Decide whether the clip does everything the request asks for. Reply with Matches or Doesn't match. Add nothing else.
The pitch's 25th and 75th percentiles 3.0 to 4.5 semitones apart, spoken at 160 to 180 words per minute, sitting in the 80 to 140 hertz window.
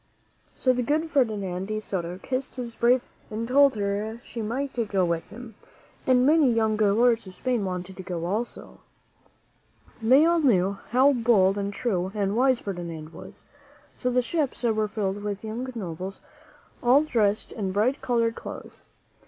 Doesn't match